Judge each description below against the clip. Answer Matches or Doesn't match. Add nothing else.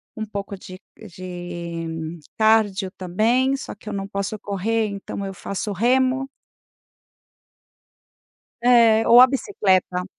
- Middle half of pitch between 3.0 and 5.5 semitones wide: Matches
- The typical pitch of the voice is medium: Doesn't match